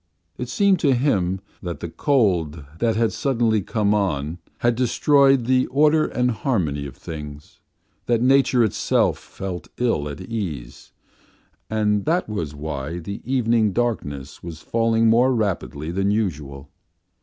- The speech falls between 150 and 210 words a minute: No, average, 140 wpm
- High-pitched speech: No, low, 105 Hz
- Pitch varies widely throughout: Yes, wide, 7.0 semitones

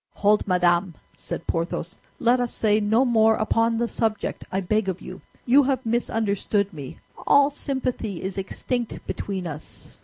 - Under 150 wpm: No, average, 155 wpm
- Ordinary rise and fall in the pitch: Yes, average, 3.9 semitones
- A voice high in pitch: Yes, high, 215 Hz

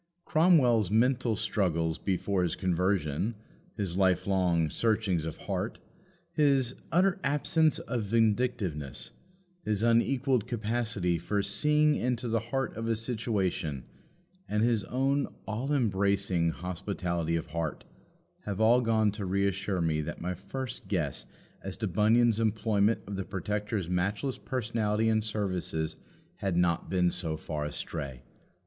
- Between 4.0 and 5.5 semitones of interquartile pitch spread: Yes, average, 4.5 semitones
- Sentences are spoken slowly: Yes, slow, 130 wpm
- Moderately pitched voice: No, low, 105 Hz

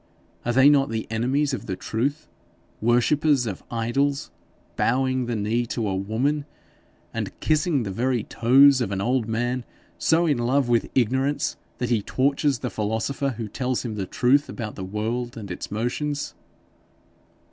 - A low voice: Yes, low, 120 Hz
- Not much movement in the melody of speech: No, average, 3.7 semitones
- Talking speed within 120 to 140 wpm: No, average, 160 wpm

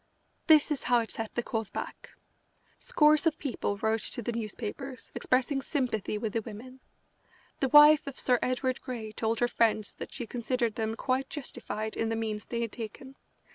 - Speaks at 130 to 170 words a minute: No, average, 180 wpm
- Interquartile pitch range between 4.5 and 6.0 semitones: No, average, 3.2 semitones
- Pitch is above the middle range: Yes, high, 240 Hz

